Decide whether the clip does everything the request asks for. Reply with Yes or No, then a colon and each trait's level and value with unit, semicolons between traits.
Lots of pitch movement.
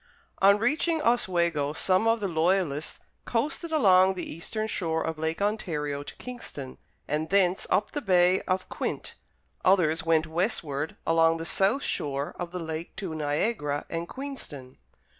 No: average, 4.4 semitones